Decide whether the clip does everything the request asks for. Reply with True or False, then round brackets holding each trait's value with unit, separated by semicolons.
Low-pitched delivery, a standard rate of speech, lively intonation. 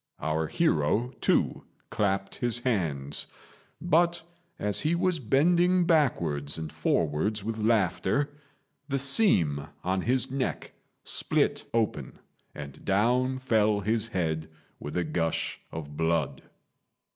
False (105 Hz; 115 wpm; 8.5 semitones)